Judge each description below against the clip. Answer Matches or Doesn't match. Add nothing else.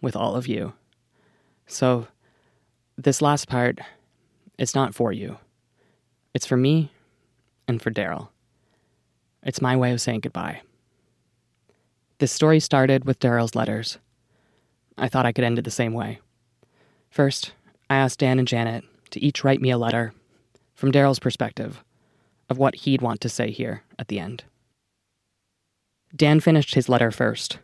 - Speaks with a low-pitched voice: Matches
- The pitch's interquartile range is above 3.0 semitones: Doesn't match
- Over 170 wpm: Doesn't match